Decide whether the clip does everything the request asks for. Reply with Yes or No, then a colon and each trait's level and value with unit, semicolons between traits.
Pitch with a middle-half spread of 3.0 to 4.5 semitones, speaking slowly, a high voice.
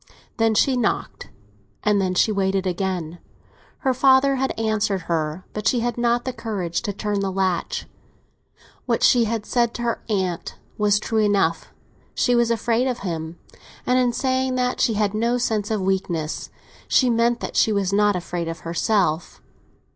No: average, 4.1 semitones; average, 170 wpm; high, 210 Hz